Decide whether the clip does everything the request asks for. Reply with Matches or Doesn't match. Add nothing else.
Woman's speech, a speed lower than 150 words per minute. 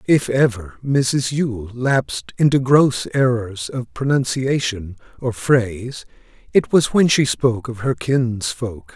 Doesn't match